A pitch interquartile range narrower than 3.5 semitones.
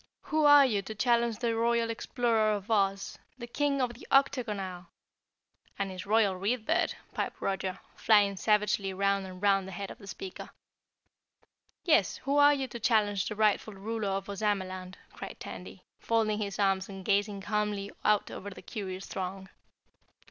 Yes: average, 2.8 semitones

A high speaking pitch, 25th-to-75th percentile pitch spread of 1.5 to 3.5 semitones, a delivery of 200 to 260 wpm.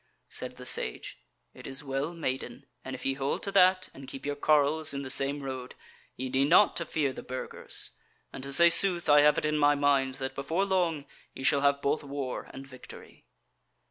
No: medium, 140 Hz; narrow, 2.6 semitones; fast, 205 wpm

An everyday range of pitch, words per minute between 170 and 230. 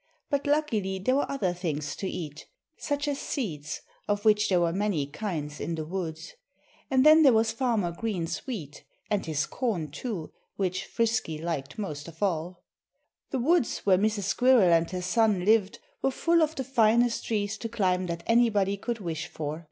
No: wide, 5.8 semitones; average, 180 wpm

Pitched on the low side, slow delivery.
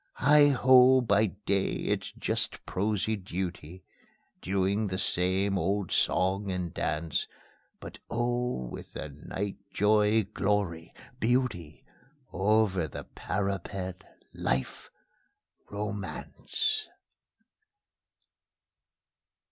Yes: low, 100 Hz; slow, 85 wpm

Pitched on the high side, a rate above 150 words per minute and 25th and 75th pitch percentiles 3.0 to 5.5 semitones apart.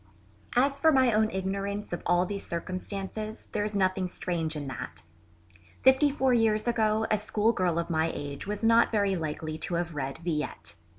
Yes: high, 195 Hz; average, 175 wpm; average, 4.4 semitones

